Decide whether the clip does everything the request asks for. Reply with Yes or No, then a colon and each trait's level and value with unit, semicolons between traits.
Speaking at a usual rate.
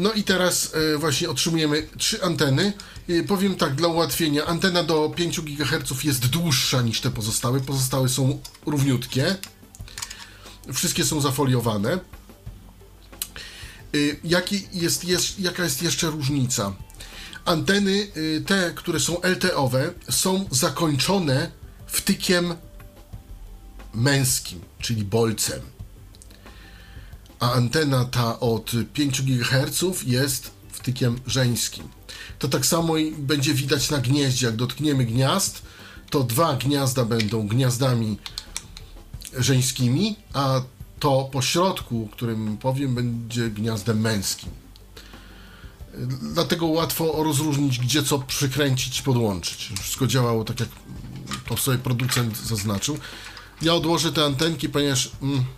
No: slow, 105 wpm